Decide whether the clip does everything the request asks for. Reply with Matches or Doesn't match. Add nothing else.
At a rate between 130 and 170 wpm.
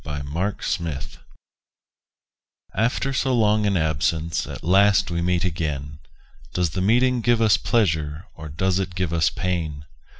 Matches